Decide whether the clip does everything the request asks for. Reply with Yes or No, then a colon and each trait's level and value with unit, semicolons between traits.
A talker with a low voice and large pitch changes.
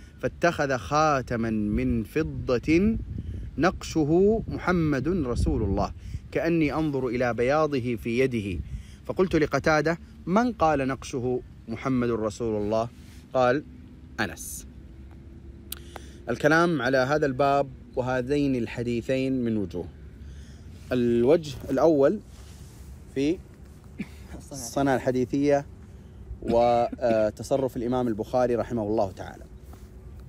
Yes: low, 120 Hz; wide, 6.2 semitones